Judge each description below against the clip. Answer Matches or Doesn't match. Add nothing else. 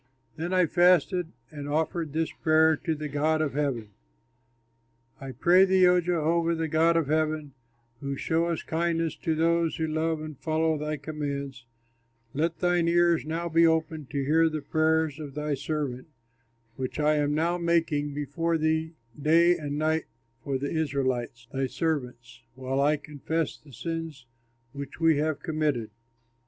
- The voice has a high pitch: Doesn't match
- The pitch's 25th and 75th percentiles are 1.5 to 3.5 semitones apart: Matches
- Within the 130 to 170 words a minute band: Matches